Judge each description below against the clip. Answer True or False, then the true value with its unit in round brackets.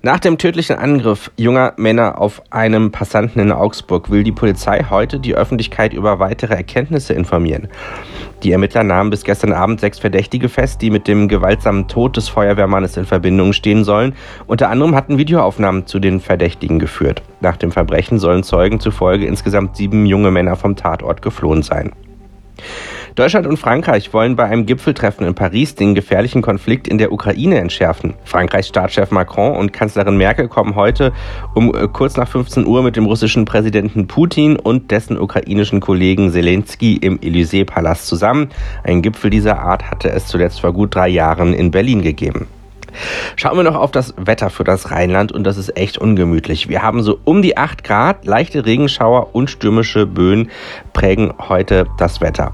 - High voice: False (105 Hz)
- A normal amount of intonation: True (3.2 semitones)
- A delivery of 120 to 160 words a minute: False (170 wpm)